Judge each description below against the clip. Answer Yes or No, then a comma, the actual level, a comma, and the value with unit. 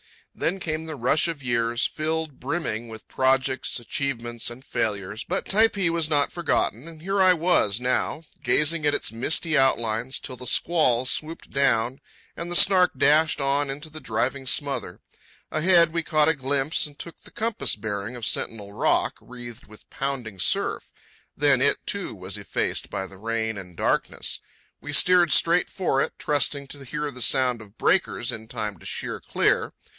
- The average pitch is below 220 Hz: Yes, low, 135 Hz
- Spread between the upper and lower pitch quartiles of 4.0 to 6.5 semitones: Yes, average, 5.3 semitones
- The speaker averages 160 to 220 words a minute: Yes, average, 170 wpm